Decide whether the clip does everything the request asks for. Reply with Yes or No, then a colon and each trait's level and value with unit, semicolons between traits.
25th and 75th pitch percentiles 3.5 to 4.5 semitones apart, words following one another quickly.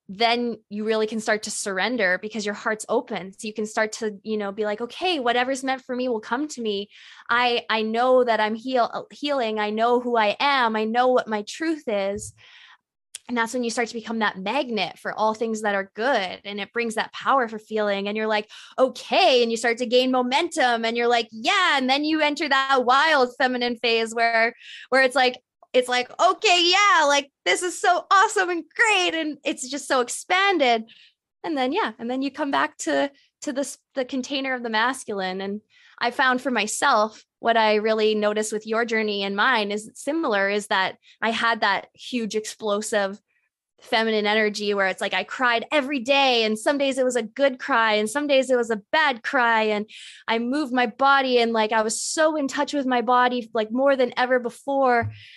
Yes: average, 4.0 semitones; fast, 210 wpm